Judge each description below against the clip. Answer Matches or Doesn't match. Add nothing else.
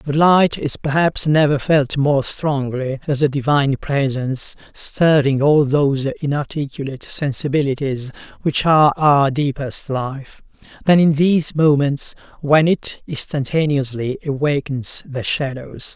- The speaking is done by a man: Matches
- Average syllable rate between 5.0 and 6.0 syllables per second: Doesn't match